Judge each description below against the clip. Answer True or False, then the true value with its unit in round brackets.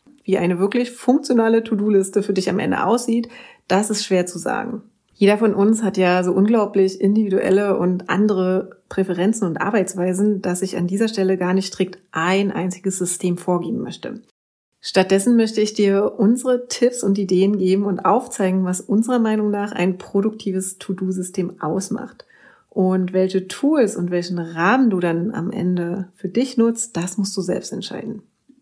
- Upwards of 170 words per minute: False (165 wpm)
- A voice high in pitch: True (195 Hz)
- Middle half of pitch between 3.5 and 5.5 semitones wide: False (2.9 semitones)